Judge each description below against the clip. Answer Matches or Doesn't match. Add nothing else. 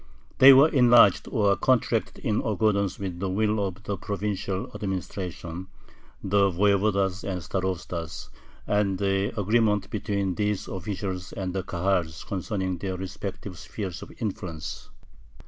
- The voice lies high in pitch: Doesn't match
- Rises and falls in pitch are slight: Matches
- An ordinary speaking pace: Doesn't match